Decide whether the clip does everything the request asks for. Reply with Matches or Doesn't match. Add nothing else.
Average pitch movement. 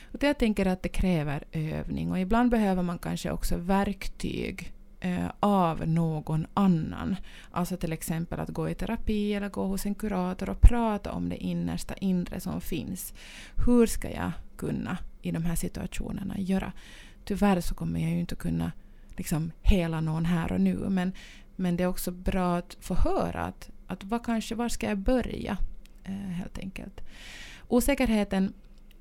Matches